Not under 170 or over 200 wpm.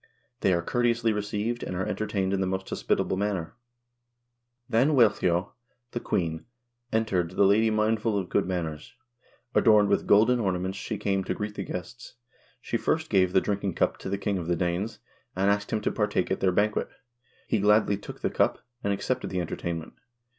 Yes: average, 185 wpm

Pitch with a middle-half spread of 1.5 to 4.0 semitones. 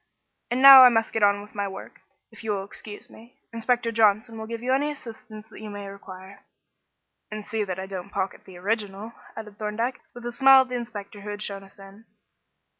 Yes: average, 2.8 semitones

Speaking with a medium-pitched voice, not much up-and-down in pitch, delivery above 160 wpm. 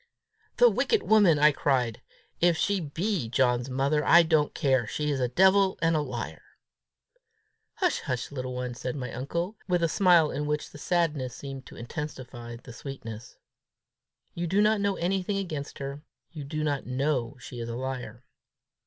No: medium, 145 Hz; average, 5.2 semitones; average, 170 wpm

